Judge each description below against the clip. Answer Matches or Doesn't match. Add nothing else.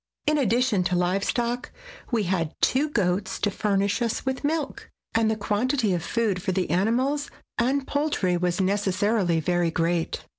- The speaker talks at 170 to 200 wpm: Doesn't match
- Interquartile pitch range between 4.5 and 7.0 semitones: Matches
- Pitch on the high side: Matches